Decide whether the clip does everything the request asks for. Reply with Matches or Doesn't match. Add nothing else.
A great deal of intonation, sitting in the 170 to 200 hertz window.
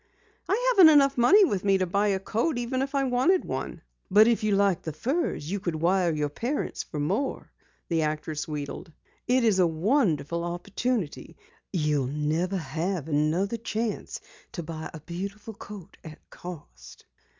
Matches